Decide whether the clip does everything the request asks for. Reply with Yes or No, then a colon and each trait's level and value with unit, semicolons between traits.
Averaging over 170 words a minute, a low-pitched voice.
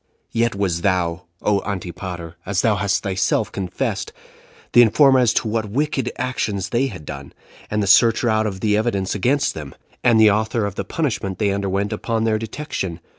Yes: average, 180 wpm; low, 105 Hz